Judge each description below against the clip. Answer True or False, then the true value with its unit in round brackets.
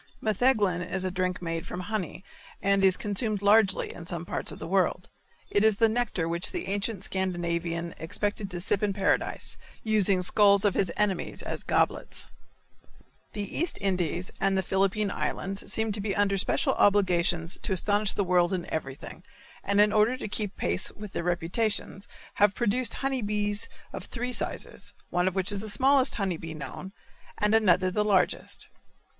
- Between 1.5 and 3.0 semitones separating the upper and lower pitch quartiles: True (2.7 semitones)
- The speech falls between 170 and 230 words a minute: True (175 wpm)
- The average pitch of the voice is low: False (195 Hz)